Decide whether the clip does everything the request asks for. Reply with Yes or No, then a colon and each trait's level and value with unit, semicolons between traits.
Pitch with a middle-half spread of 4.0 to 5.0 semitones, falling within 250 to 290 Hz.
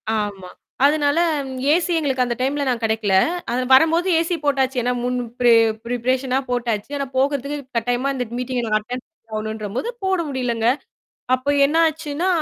No: average, 3.3 semitones; very high, 255 Hz